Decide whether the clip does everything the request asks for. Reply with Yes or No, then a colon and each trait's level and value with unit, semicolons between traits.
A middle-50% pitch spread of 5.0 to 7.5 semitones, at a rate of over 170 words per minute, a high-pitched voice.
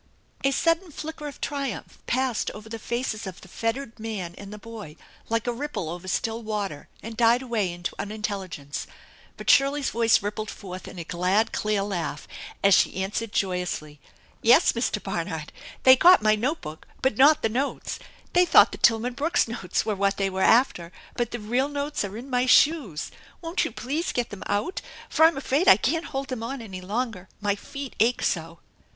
Yes: average, 5.3 semitones; average, 190 wpm; high, 225 Hz